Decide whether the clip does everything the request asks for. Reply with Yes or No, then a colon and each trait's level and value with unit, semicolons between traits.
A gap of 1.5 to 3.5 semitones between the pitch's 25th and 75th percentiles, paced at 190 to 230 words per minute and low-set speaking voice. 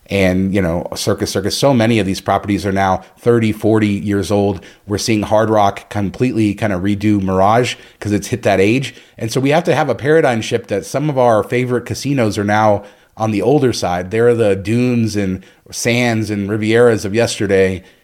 Yes: average, 3.0 semitones; average, 200 wpm; low, 105 Hz